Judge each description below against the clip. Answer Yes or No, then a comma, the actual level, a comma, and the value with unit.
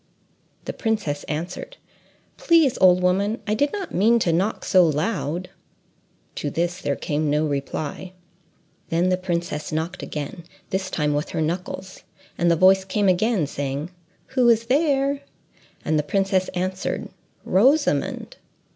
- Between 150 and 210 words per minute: No, average, 140 wpm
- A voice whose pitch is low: No, medium, 185 Hz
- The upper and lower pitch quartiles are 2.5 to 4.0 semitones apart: No, wide, 5.4 semitones